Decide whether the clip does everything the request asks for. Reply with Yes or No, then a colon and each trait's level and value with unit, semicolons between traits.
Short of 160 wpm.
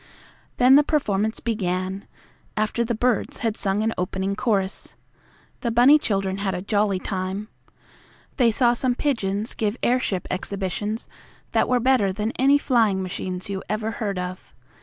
Yes: average, 150 wpm